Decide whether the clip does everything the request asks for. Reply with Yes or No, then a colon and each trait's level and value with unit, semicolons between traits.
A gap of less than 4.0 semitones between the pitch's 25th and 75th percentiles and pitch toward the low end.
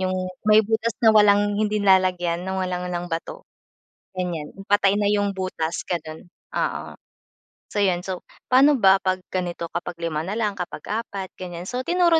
No: average, 2.9 semitones; high, 190 Hz